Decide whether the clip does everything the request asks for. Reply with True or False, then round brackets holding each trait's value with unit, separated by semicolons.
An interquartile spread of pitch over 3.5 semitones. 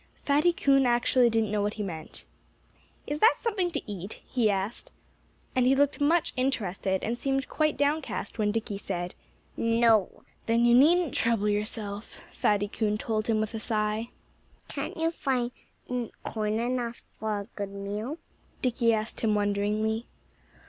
True (3.9 semitones)